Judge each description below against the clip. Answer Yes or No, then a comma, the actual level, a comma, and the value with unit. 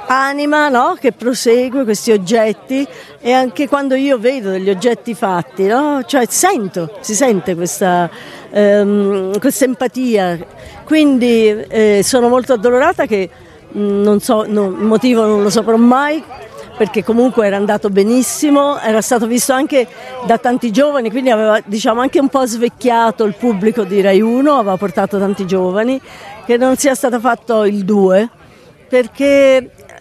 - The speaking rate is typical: Yes, average, 150 wpm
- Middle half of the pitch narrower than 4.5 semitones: Yes, average, 4.0 semitones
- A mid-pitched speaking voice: No, high, 230 Hz